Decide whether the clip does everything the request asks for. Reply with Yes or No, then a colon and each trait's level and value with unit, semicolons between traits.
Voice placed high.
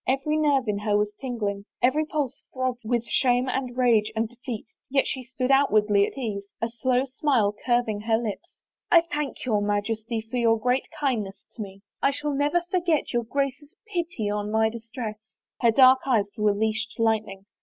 Yes: high, 235 Hz